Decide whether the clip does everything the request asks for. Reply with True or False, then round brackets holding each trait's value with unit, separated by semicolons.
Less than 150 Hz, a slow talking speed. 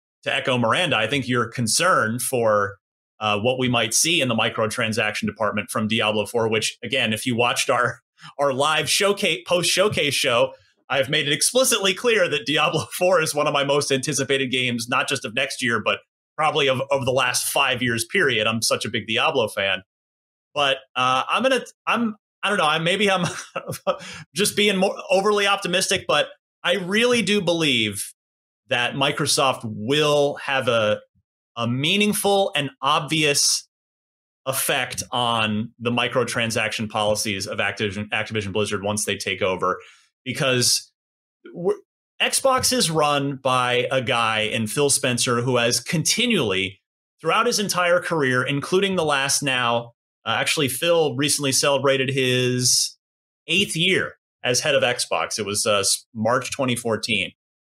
False (135 Hz; 155 wpm)